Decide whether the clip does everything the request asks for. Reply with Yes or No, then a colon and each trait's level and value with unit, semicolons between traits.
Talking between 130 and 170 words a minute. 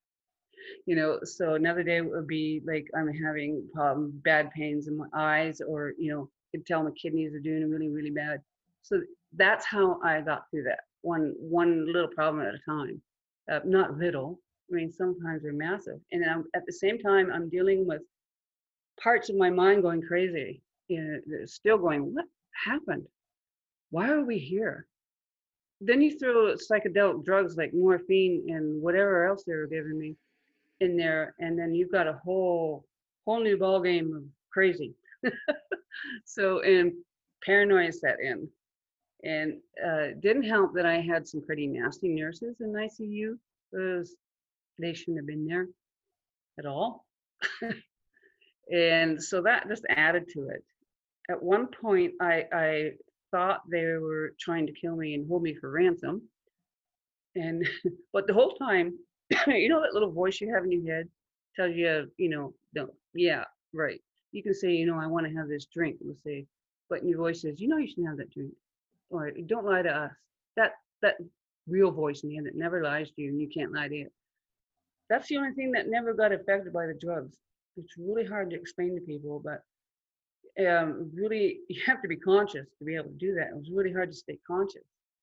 No: average, 185 wpm